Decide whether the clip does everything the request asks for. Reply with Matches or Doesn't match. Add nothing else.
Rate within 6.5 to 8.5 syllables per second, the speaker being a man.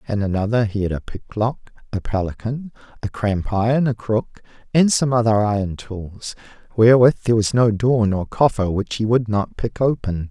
Doesn't match